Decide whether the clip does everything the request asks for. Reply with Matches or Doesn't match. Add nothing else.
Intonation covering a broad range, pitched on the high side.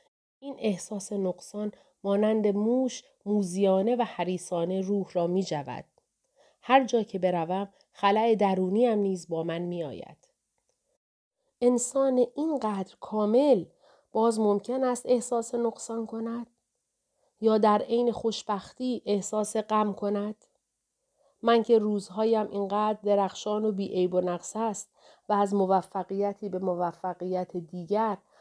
Doesn't match